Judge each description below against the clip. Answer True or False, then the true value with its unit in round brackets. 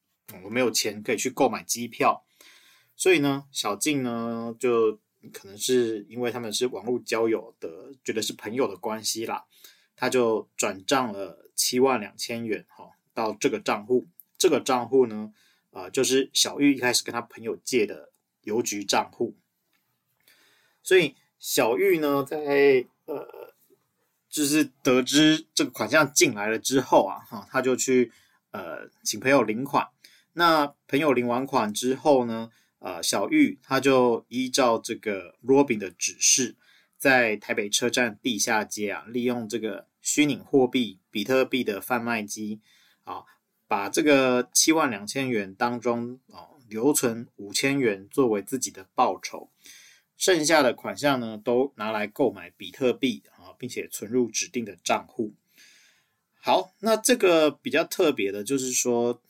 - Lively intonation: False (3.8 semitones)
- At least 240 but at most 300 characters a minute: False (225 characters per minute)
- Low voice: True (125 Hz)